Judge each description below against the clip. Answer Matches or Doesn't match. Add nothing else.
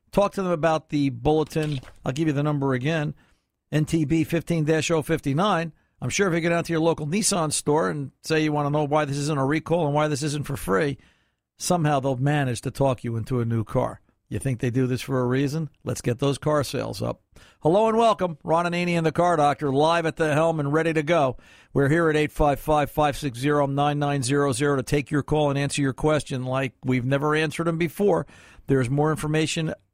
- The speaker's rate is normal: Doesn't match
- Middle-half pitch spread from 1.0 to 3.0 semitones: Matches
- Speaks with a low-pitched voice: Doesn't match